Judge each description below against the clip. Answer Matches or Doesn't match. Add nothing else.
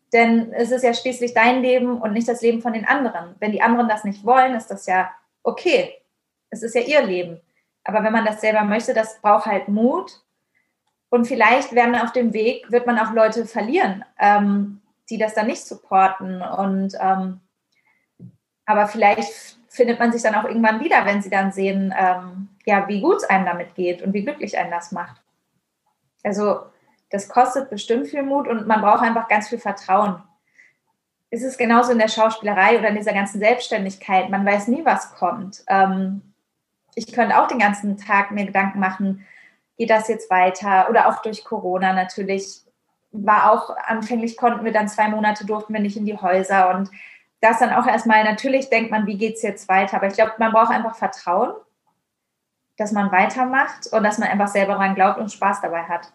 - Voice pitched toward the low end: Doesn't match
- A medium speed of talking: Doesn't match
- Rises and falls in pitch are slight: Doesn't match